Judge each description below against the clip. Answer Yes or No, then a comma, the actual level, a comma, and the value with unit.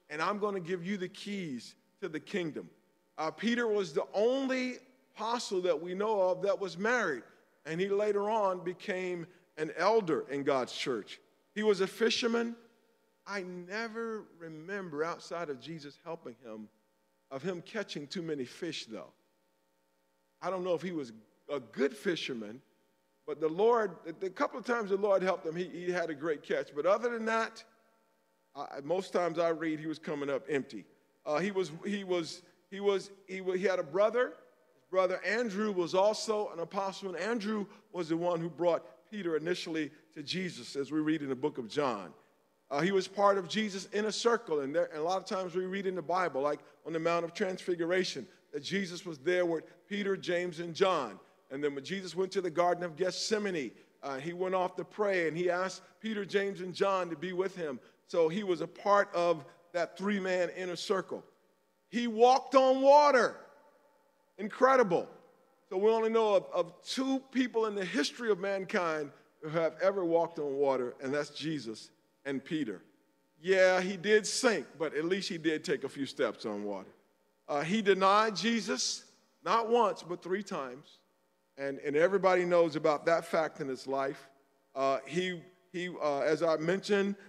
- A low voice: No, medium, 185 Hz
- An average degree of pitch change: Yes, average, 4.3 semitones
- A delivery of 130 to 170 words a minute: No, average, 190 wpm